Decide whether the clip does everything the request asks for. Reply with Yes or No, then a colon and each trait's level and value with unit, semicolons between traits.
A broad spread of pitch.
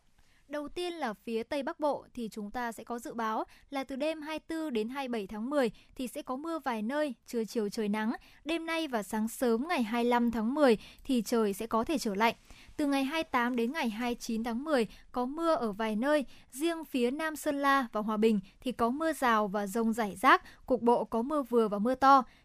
No: average, 4.5 semitones